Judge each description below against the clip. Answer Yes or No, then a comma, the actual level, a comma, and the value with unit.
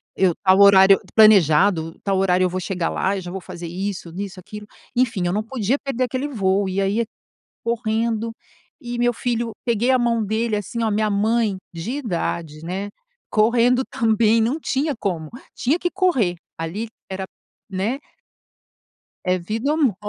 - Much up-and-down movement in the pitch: No, average, 3.9 semitones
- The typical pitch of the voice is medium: No, high, 210 Hz